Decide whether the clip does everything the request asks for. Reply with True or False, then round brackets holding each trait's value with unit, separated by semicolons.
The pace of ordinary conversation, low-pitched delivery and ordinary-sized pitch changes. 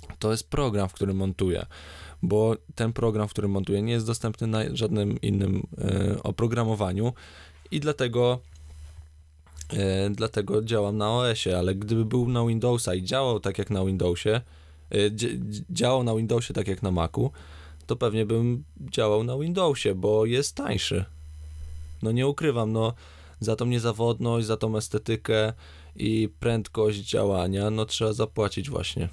True (140 wpm; 105 Hz; 3.7 semitones)